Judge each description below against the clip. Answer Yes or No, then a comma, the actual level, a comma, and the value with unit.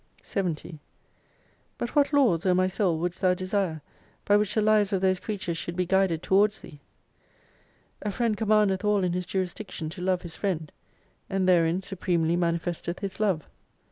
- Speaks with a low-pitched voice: No, medium, 185 Hz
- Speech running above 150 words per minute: Yes, average, 175 wpm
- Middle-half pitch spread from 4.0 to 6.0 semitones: No, average, 3.0 semitones